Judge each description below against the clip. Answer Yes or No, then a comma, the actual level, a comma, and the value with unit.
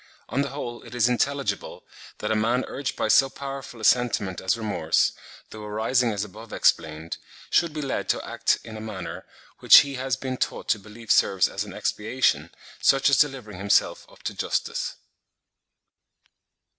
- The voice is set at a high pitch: No, low, 115 Hz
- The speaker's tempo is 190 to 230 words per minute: No, average, 170 wpm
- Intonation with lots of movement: No, average, 4.1 semitones